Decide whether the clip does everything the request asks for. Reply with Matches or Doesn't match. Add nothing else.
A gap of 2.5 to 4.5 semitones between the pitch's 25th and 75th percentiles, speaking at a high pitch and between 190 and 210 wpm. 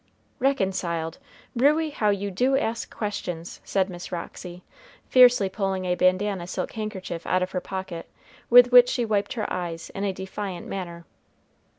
Doesn't match